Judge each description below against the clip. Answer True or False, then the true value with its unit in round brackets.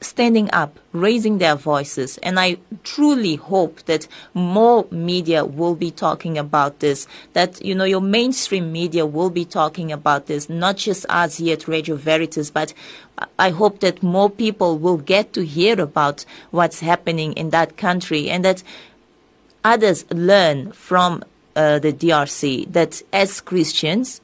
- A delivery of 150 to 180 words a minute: True (160 wpm)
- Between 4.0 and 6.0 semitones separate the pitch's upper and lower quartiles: False (3.3 semitones)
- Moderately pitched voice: True (175 Hz)